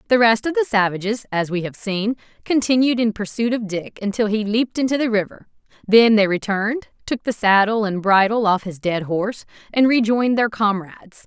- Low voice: No, high, 215 Hz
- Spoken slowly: No, average, 190 wpm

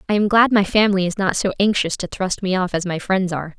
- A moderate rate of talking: No, fast, 285 wpm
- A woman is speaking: Yes, female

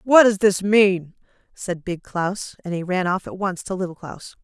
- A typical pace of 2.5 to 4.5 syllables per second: Yes, 4.4 syllables/s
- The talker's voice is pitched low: No, high, 190 Hz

